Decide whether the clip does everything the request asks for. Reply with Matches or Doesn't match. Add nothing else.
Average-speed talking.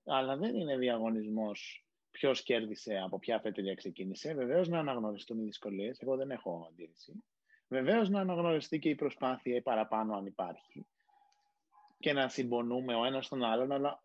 Matches